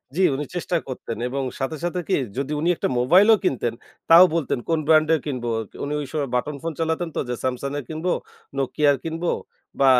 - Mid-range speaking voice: Yes, medium, 155 Hz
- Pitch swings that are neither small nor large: Yes, average, 3.5 semitones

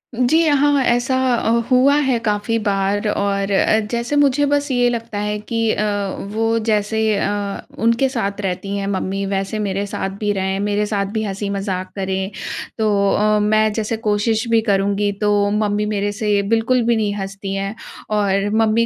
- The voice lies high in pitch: Yes, high, 210 Hz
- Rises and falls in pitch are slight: Yes, narrow, 2.3 semitones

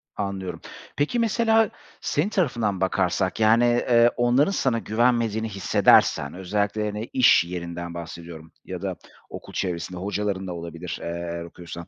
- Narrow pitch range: No, wide, 5.6 semitones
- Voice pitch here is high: No, low, 100 Hz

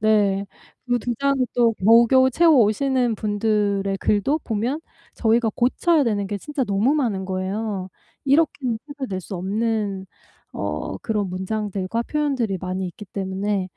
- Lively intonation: No, average, 4.1 semitones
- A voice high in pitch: Yes, high, 215 Hz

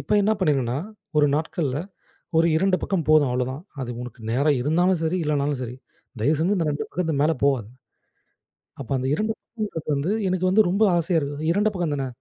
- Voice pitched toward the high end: No, medium, 155 Hz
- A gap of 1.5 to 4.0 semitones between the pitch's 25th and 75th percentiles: No, average, 4.4 semitones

